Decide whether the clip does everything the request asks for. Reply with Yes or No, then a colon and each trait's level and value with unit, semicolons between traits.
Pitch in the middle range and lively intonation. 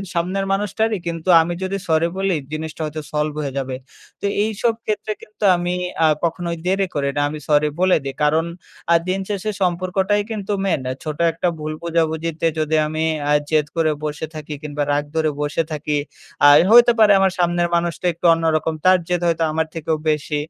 No: medium, 165 Hz; average, 3.3 semitones